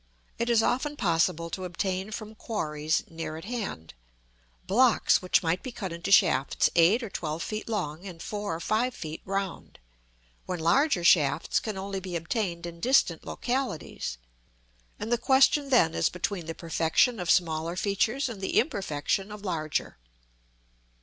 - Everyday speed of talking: Yes, average, 155 wpm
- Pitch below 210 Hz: Yes, medium, 185 Hz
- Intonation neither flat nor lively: Yes, average, 5.0 semitones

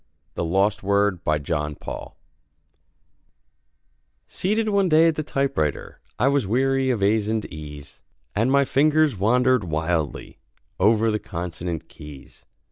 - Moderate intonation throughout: No, wide, 8.2 semitones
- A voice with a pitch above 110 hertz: No, low, 105 Hz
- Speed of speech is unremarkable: No, slow, 130 wpm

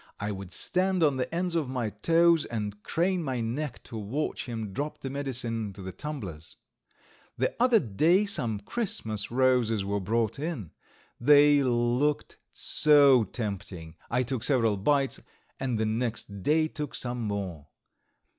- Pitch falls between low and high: No, low, 125 Hz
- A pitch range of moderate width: No, wide, 5.8 semitones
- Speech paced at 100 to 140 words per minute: No, average, 150 wpm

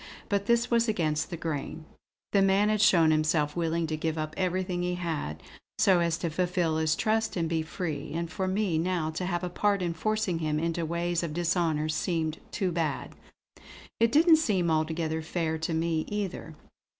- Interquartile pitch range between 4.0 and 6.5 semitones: No, average, 2.8 semitones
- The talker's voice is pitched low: No, medium, 170 Hz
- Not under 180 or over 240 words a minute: Yes, average, 185 wpm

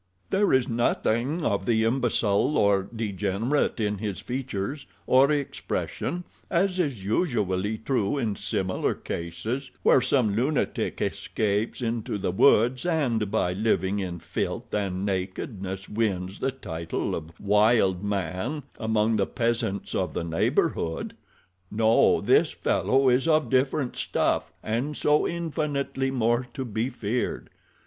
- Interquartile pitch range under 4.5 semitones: No, average, 5.1 semitones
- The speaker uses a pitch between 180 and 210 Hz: No, low, 110 Hz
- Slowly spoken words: Yes, slow, 125 wpm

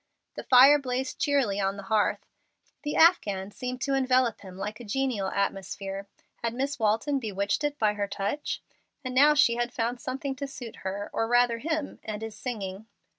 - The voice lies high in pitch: Yes, high, 235 Hz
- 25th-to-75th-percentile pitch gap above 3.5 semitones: Yes, average, 4.8 semitones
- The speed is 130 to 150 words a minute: No, average, 180 wpm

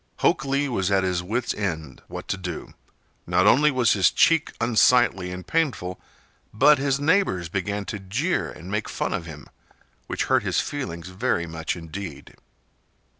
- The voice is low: Yes, low, 100 Hz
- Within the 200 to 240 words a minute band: No, average, 165 wpm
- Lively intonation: Yes, wide, 6.6 semitones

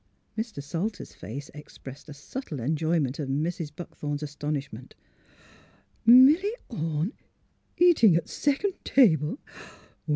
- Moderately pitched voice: Yes, medium, 160 Hz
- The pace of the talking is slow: Yes, slow, 105 wpm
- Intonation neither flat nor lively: No, wide, 7.8 semitones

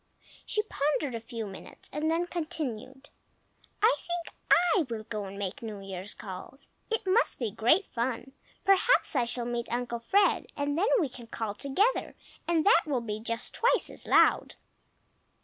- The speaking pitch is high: Yes, very high, 260 Hz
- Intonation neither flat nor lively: No, wide, 7.2 semitones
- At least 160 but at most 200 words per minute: Yes, average, 165 wpm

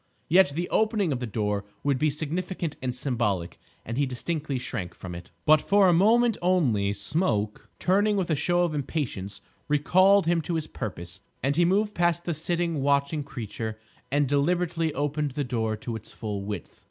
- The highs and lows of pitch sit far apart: Yes, wide, 7.1 semitones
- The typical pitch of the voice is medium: Yes, medium, 145 Hz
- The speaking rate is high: No, average, 180 wpm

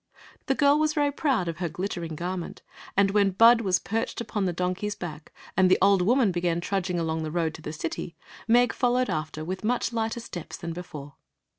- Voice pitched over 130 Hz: Yes, medium, 185 Hz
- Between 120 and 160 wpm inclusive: No, fast, 205 wpm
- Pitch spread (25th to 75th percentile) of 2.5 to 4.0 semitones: No, average, 5.2 semitones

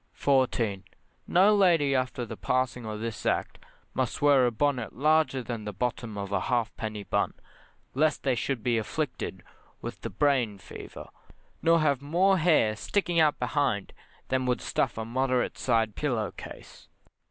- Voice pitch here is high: No, low, 125 Hz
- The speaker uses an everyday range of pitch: Yes, average, 4.7 semitones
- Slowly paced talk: No, average, 155 wpm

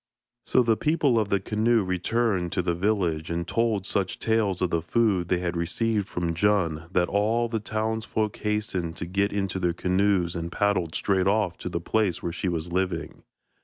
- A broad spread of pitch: No, average, 3.7 semitones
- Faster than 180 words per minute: Yes, average, 190 wpm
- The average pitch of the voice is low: Yes, very low, 95 Hz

